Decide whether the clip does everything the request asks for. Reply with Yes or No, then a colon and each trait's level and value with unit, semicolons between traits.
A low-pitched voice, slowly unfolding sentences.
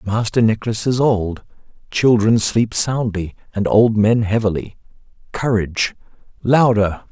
Yes: low, 110 Hz; slow, 110 wpm